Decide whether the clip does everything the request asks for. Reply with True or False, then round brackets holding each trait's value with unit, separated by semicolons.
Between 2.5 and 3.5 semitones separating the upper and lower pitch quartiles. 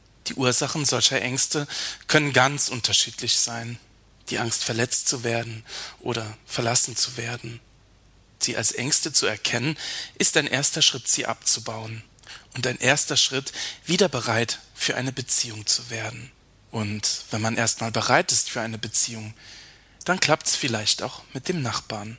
True (2.8 semitones)